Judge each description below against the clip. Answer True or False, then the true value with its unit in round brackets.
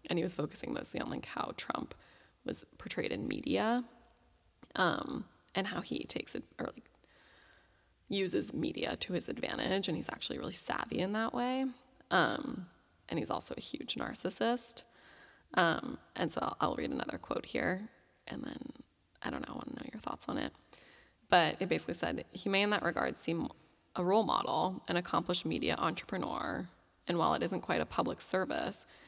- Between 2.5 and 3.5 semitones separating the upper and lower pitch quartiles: False (4.6 semitones)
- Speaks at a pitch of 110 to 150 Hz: False (235 Hz)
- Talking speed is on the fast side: False (180 wpm)